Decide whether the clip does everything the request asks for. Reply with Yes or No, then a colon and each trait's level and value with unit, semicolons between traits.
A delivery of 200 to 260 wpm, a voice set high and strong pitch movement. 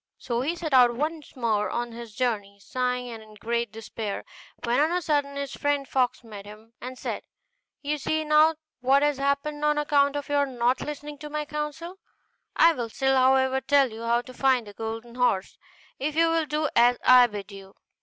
No: fast, 205 wpm; very high, 260 Hz; average, 4.0 semitones